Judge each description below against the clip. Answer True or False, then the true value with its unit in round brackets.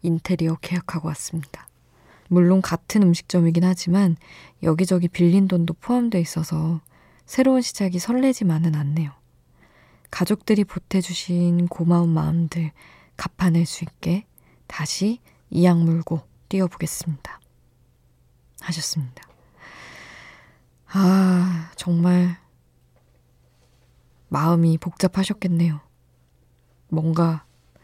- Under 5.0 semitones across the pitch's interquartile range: True (2.4 semitones)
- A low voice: False (170 Hz)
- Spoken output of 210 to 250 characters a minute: True (230 characters per minute)